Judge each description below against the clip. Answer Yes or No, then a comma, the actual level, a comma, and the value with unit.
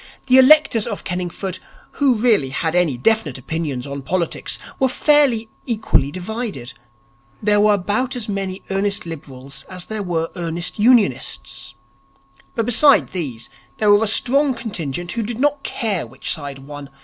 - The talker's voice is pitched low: No, high, 195 Hz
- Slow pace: No, average, 150 wpm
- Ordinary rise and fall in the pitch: No, wide, 6.4 semitones